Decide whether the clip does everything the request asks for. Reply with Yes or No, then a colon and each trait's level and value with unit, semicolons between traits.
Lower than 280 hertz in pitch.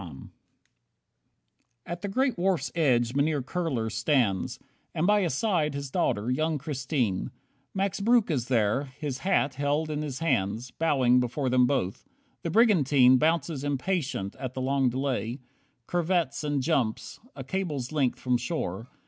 Yes: medium, 140 Hz